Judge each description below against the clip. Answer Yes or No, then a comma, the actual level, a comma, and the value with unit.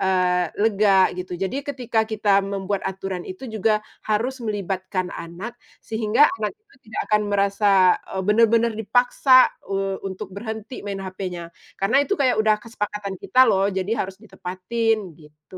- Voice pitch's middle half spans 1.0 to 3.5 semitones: Yes, average, 2.9 semitones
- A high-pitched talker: Yes, high, 205 Hz